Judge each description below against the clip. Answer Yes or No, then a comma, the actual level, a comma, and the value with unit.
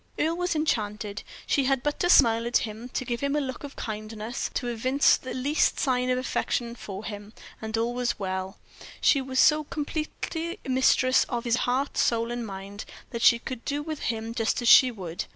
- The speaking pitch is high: Yes, high, 245 Hz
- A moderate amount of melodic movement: Yes, average, 3.8 semitones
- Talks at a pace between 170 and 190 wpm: No, average, 200 wpm